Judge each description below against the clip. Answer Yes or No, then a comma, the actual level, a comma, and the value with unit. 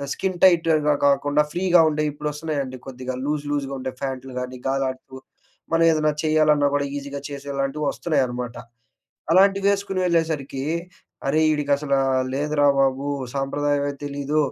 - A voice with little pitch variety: Yes, narrow, 2.2 semitones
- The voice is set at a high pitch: No, medium, 145 Hz